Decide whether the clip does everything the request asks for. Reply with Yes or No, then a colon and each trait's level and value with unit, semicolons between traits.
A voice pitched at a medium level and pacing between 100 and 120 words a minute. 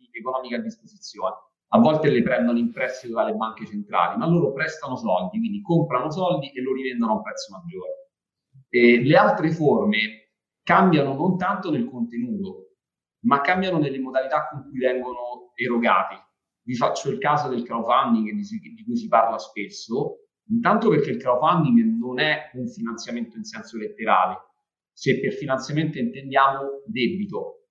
No: medium, 155 Hz; average, 150 wpm